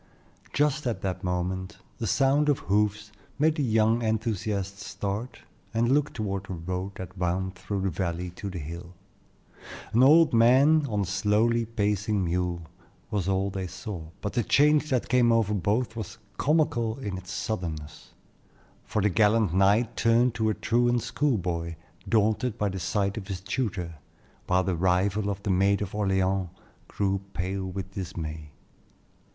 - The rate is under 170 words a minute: Yes, average, 160 wpm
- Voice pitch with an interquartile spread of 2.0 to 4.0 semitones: Yes, average, 3.7 semitones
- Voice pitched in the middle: No, low, 100 Hz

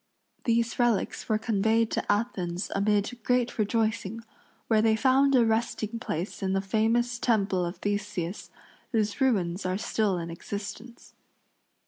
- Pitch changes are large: No, average, 2.9 semitones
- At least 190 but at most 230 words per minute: No, slow, 135 wpm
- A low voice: No, high, 215 Hz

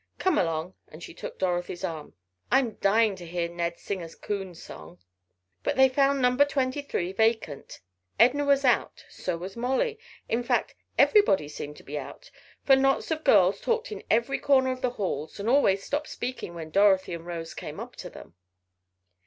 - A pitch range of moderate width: No, wide, 7.5 semitones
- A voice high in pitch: Yes, high, 210 Hz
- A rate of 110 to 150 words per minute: No, average, 185 wpm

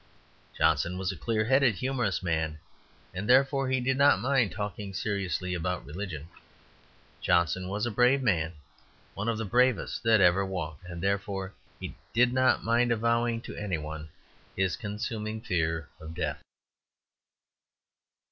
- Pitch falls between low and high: No, low, 100 Hz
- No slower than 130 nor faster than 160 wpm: Yes, average, 145 wpm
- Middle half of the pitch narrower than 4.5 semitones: No, average, 5.1 semitones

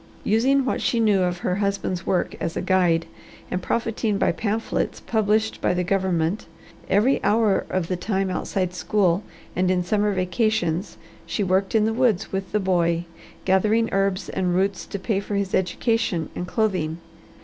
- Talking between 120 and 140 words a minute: No, average, 170 wpm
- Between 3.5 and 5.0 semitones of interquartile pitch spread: No, average, 3.0 semitones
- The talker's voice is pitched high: Yes, high, 195 Hz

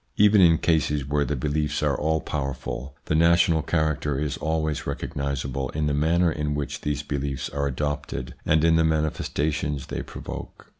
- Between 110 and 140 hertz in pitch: No, very low, 75 Hz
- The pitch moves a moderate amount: No, narrow, 1.9 semitones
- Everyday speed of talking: Yes, average, 165 wpm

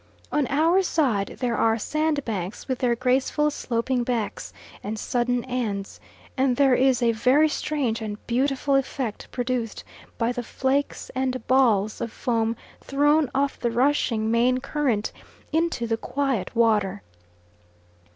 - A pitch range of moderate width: Yes, average, 3.2 semitones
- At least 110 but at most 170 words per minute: Yes, slow, 135 wpm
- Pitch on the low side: No, very high, 250 Hz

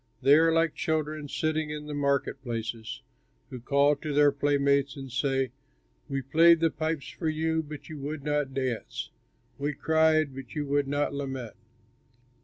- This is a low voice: No, medium, 145 Hz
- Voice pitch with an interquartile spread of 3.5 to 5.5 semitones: No, narrow, 2.5 semitones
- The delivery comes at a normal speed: Yes, average, 165 wpm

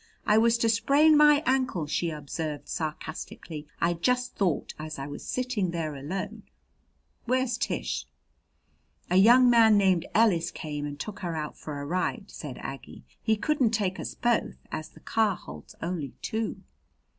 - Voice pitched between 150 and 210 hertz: Yes, medium, 185 Hz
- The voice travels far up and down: Yes, wide, 7.1 semitones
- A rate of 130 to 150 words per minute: No, average, 165 wpm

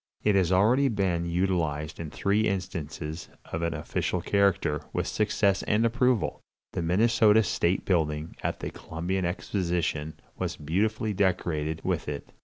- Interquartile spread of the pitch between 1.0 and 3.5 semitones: No, average, 4.2 semitones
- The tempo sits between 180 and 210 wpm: No, average, 140 wpm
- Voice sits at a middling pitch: No, very low, 90 Hz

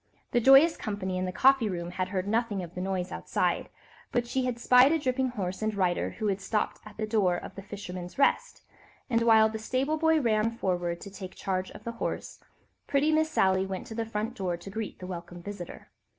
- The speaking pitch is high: Yes, high, 210 Hz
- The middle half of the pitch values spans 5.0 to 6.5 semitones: No, average, 4.3 semitones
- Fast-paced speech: Yes, fast, 220 wpm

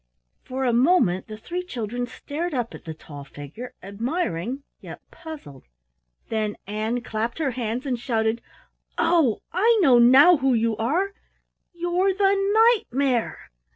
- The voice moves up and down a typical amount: No, wide, 7.5 semitones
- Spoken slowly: No, average, 145 wpm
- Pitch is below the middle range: No, very high, 250 Hz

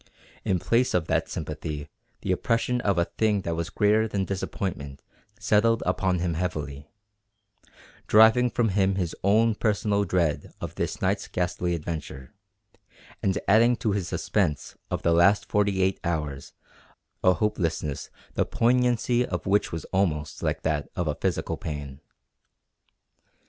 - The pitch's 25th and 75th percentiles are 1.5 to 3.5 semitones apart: No, average, 4.6 semitones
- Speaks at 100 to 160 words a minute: Yes, average, 145 wpm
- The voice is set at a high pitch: No, very low, 95 Hz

